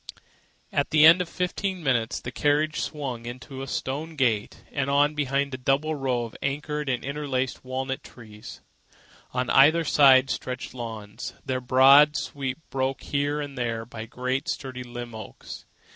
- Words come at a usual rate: Yes, average, 160 wpm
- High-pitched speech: No, low, 135 Hz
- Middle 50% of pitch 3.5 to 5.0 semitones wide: No, narrow, 2.6 semitones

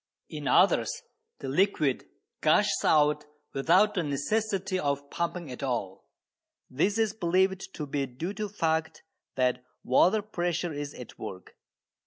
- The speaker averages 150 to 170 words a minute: No, average, 140 wpm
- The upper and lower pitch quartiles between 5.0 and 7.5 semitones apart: Yes, wide, 5.5 semitones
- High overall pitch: No, medium, 160 Hz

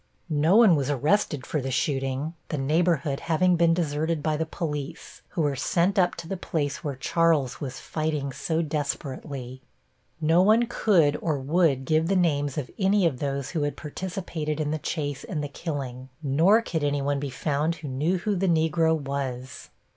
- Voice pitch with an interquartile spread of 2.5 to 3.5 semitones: Yes, average, 3.2 semitones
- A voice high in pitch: No, medium, 150 Hz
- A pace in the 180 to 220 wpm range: Yes, average, 185 wpm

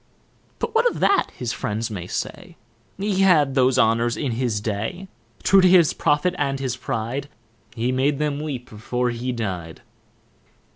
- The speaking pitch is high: No, low, 130 Hz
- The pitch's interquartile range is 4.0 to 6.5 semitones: Yes, average, 4.6 semitones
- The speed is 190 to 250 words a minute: No, average, 160 wpm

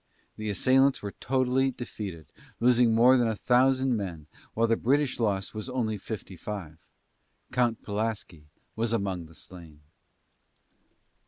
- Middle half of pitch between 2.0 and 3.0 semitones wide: No, average, 4.3 semitones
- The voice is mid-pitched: No, low, 110 Hz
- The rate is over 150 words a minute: No, slow, 135 wpm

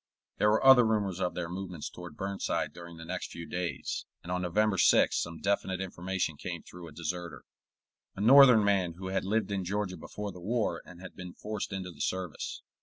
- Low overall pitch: Yes, very low, 95 Hz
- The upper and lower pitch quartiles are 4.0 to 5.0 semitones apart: No, average, 2.7 semitones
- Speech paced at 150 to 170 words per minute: No, average, 200 wpm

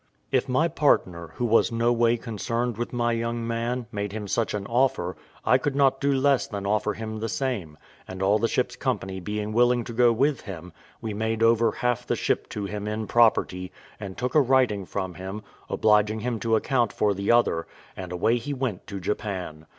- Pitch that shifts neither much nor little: Yes, average, 3.3 semitones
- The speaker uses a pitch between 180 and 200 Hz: No, low, 110 Hz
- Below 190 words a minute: No, fast, 205 wpm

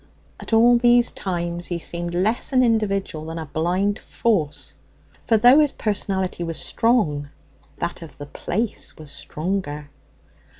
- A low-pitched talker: No, medium, 185 Hz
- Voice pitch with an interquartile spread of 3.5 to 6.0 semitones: Yes, wide, 5.6 semitones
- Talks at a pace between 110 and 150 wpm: Yes, average, 140 wpm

